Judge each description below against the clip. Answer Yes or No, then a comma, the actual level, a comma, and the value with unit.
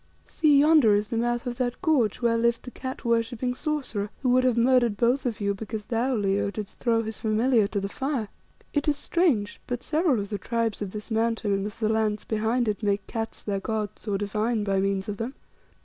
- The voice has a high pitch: Yes, high, 225 Hz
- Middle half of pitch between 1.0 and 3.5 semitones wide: Yes, average, 3.1 semitones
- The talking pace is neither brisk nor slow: No, fast, 220 wpm